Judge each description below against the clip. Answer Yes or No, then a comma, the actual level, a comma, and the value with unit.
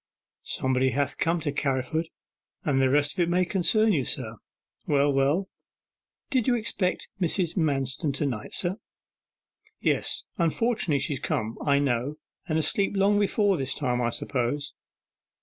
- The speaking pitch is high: No, medium, 150 Hz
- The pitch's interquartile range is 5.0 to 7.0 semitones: Yes, average, 5.3 semitones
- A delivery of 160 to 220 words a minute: No, average, 150 wpm